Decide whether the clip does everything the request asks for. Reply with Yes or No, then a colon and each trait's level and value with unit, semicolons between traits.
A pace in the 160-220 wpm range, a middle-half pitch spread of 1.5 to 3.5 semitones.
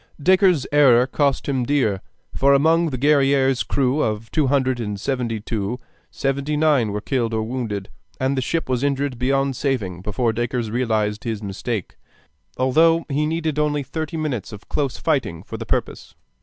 No: average, 170 wpm; average, 4.2 semitones